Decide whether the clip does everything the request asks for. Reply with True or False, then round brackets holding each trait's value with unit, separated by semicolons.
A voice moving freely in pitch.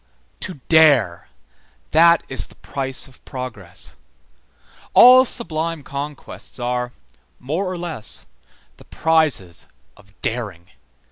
True (5.9 semitones)